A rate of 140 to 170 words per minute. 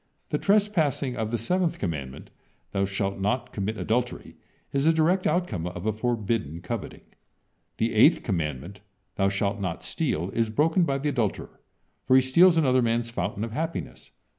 Yes: average, 165 wpm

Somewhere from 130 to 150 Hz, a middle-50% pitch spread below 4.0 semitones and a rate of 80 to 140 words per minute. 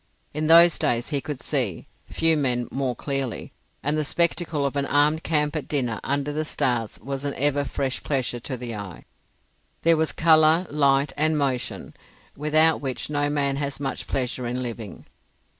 No: medium, 140 Hz; average, 3.0 semitones; average, 165 wpm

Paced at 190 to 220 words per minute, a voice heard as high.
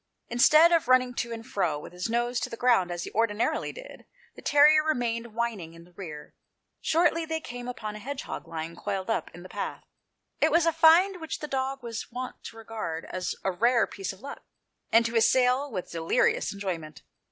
Yes: average, 200 wpm; high, 235 Hz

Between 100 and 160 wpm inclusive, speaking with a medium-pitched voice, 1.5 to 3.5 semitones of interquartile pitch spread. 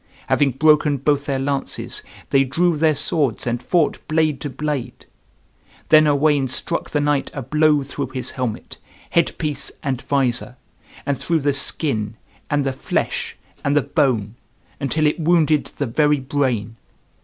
Yes: average, 155 wpm; medium, 145 Hz; narrow, 2.5 semitones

